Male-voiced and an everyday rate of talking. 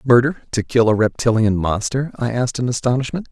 Yes: male; average, 180 wpm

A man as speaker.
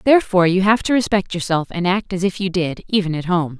No: female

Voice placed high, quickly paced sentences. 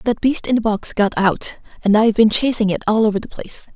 Yes: high, 215 Hz; fast, 255 wpm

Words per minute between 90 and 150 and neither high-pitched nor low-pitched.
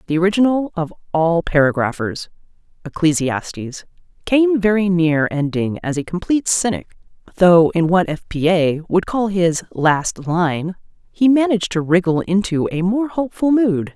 Yes: slow, 135 wpm; medium, 180 Hz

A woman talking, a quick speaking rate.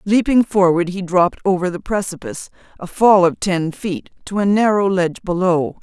No: female; average, 175 wpm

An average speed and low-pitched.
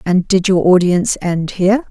No: average, 190 wpm; medium, 185 Hz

